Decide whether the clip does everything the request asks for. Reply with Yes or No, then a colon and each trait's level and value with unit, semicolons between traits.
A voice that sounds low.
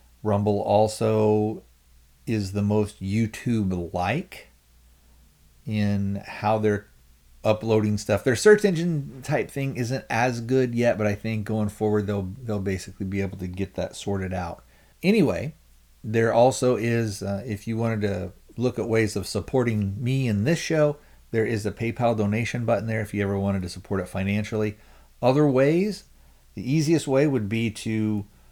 Yes: low, 105 Hz